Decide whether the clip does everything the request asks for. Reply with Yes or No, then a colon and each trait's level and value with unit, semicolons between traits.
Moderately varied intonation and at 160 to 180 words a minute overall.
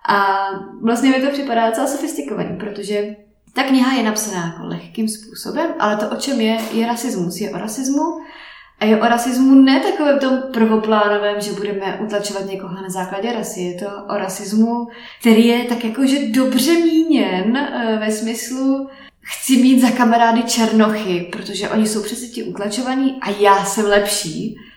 Yes: average, 4.1 semitones; average, 165 wpm